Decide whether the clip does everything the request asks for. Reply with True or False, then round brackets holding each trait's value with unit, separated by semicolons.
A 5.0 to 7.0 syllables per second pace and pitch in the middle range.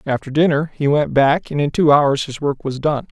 True (5.1 syllables/s; 145 Hz)